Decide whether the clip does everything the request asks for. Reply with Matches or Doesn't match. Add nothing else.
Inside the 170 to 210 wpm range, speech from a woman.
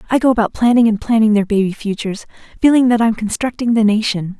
Matches